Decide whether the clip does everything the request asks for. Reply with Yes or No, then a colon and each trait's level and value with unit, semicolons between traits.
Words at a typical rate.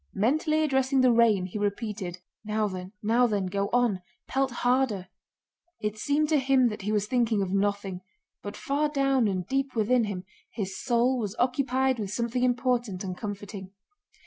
Yes: average, 170 wpm